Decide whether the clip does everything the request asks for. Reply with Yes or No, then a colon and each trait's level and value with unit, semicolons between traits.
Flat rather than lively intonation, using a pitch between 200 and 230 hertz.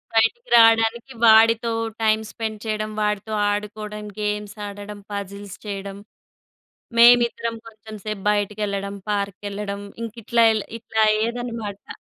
Yes: narrow, 1.8 semitones; high, 215 Hz